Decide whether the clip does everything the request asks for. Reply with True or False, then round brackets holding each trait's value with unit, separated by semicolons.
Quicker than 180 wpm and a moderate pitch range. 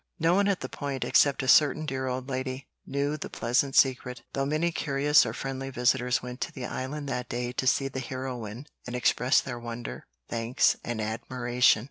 False (190 wpm; 2.2 semitones)